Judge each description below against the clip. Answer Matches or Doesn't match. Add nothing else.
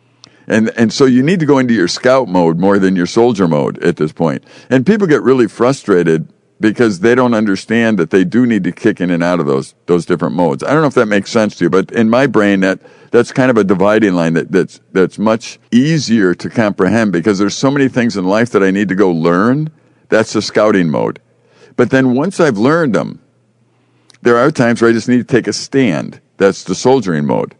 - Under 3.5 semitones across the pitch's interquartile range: Doesn't match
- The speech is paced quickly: Matches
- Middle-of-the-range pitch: Doesn't match